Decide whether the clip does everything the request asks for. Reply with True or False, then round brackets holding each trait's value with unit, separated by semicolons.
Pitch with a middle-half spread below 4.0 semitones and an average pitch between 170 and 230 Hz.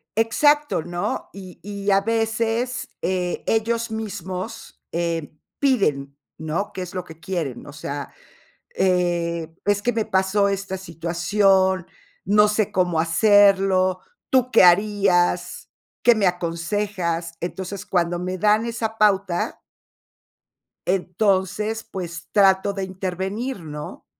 True (3.3 semitones; 190 Hz)